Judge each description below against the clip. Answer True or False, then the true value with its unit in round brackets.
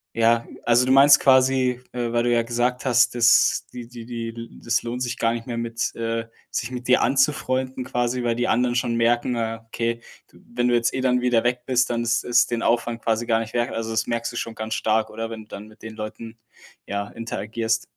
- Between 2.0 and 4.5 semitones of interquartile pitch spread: False (1.3 semitones)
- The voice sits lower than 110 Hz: False (120 Hz)